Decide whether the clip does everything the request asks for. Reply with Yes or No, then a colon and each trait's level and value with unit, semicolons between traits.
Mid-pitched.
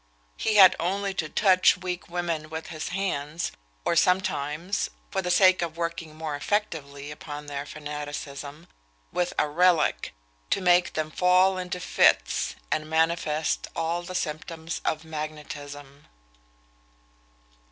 Yes: medium, 165 Hz